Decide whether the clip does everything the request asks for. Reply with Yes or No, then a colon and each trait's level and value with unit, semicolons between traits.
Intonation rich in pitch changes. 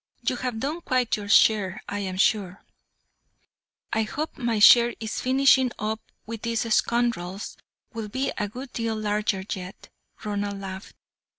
No: average, 3.0 semitones